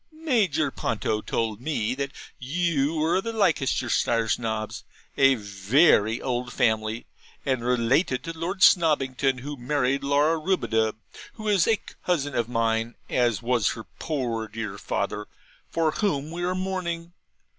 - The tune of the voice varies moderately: No, wide, 6.4 semitones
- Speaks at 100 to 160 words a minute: Yes, average, 140 wpm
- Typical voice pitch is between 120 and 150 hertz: Yes, low, 135 Hz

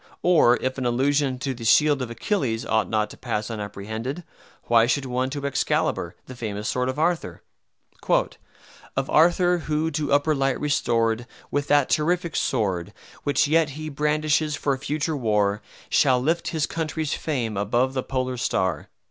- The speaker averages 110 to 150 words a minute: No, average, 160 wpm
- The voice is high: No, low, 135 Hz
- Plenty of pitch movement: No, average, 4.8 semitones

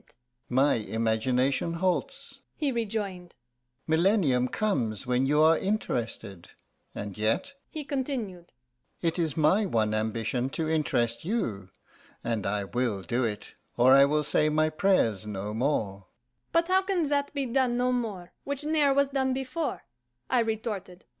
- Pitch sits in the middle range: Yes, medium, 155 Hz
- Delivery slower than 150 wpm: Yes, average, 140 wpm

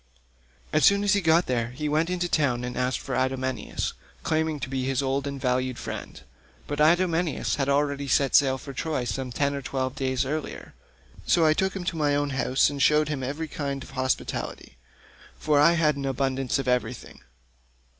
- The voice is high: No, medium, 140 Hz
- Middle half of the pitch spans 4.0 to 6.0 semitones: No, average, 2.9 semitones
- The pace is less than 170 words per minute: No, average, 195 wpm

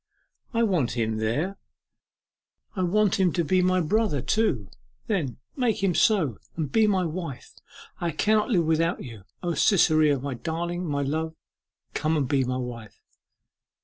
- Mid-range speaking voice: Yes, medium, 165 Hz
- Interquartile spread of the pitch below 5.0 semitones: No, wide, 5.5 semitones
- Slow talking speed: No, average, 155 wpm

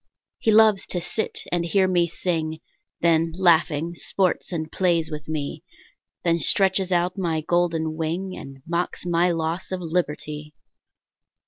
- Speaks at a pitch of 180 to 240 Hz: No, medium, 170 Hz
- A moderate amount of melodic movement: No, narrow, 2.2 semitones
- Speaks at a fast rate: No, average, 140 wpm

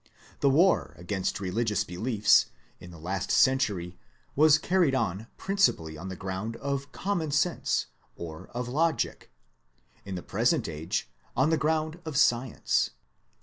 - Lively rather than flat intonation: Yes, wide, 8.5 semitones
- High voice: No, low, 120 Hz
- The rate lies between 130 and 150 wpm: Yes, average, 140 wpm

